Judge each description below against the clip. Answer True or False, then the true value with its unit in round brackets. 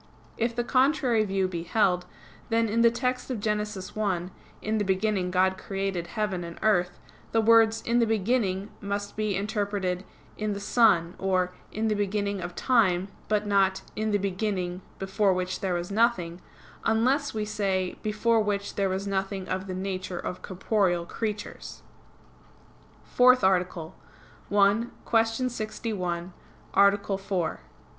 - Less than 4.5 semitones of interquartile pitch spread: True (2.8 semitones)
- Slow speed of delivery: False (150 wpm)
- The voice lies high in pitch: True (200 Hz)